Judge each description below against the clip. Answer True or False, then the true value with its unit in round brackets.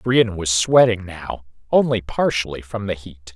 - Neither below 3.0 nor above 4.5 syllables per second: True (4.3 syllables/s)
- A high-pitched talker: False (100 Hz)